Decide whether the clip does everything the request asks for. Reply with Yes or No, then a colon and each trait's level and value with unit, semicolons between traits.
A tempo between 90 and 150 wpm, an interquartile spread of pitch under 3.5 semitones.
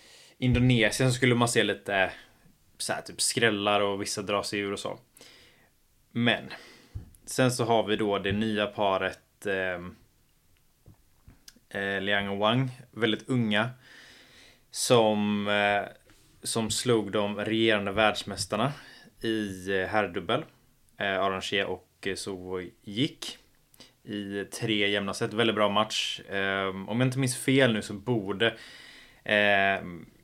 Yes: slow, 125 wpm; average, 2.8 semitones